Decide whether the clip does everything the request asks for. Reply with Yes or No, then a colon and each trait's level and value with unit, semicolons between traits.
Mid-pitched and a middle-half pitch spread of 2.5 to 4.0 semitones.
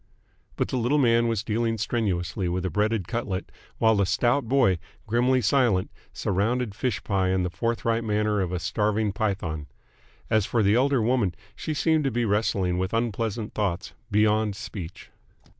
No: low, 105 Hz; average, 3.5 semitones